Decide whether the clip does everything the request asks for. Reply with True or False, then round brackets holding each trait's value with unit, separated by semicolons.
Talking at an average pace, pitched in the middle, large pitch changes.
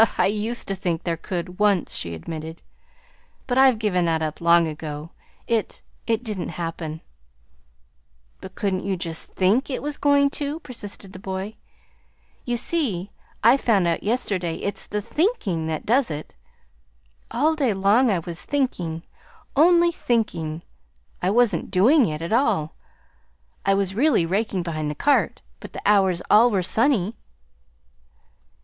False (150 wpm; 195 Hz; 6.1 semitones)